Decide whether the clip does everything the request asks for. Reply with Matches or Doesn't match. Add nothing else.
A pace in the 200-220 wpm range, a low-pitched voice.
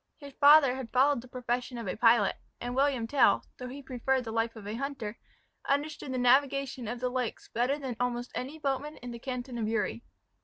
Doesn't match